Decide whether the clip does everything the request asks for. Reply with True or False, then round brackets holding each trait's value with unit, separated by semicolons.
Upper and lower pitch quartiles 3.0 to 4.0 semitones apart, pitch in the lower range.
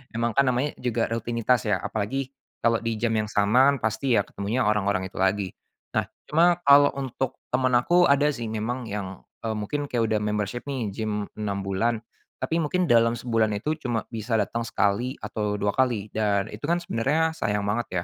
True (3.6 semitones; 115 Hz)